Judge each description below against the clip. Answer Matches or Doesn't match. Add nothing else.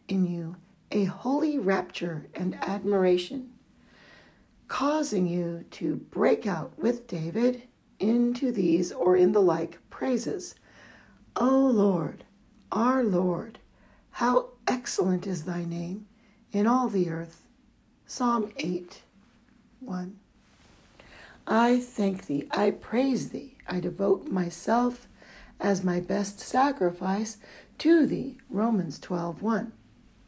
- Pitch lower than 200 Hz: Doesn't match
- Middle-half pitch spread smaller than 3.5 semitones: Doesn't match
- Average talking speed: Doesn't match